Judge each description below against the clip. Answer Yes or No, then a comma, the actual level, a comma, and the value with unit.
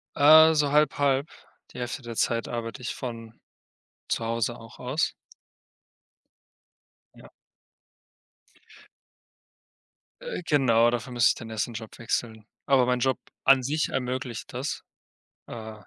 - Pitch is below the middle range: Yes, low, 125 Hz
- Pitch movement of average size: Yes, average, 3.0 semitones